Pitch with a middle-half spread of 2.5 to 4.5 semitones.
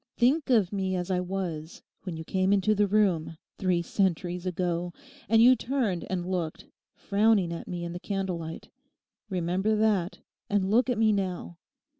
Yes: average, 3.2 semitones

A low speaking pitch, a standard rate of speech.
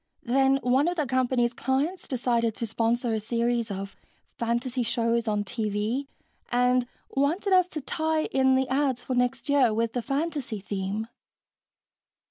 No: high, 245 Hz; average, 150 wpm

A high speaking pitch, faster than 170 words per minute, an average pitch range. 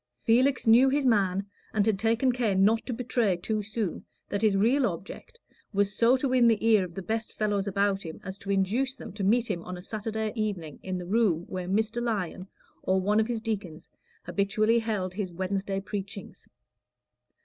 Yes: high, 210 Hz; average, 195 wpm; average, 3.0 semitones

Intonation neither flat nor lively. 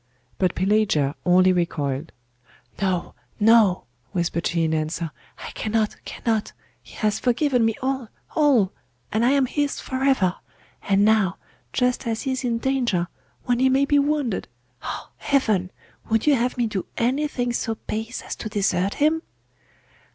No: wide, 5.7 semitones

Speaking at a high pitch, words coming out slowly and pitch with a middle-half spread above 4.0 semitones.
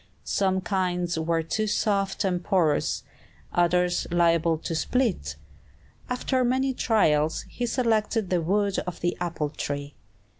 No: medium, 180 Hz; slow, 125 wpm; average, 4.4 semitones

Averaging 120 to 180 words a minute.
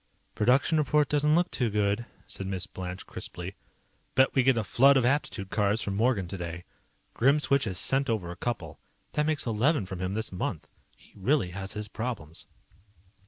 Yes: average, 175 wpm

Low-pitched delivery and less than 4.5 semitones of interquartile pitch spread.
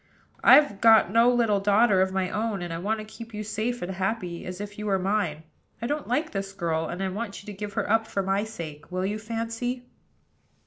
No: high, 205 Hz; average, 3.1 semitones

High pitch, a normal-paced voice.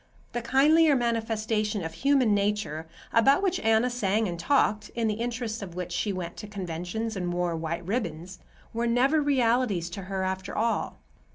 Yes: high, 215 Hz; average, 170 wpm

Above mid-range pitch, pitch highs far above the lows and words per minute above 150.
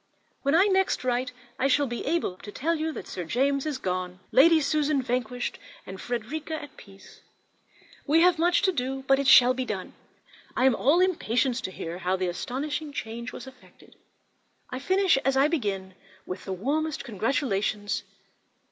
Yes: very high, 260 Hz; wide, 5.9 semitones; average, 175 wpm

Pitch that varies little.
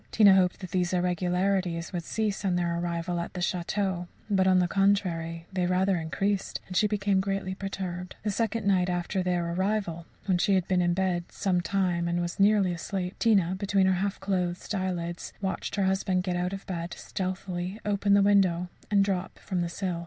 Yes: narrow, 1.9 semitones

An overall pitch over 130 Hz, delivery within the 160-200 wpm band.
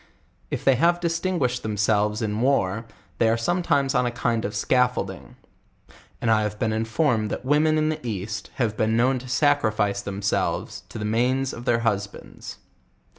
No: low, 115 Hz; average, 175 wpm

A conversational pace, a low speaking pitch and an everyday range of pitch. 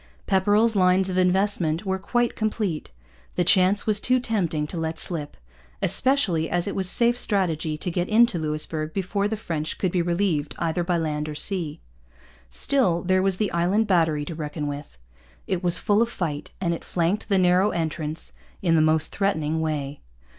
No: average, 180 wpm; medium, 175 Hz; average, 3.9 semitones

